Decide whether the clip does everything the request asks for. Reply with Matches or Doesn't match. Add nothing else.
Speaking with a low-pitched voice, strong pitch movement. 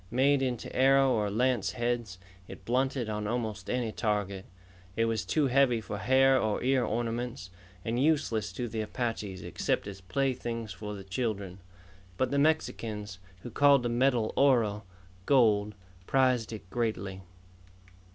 Doesn't match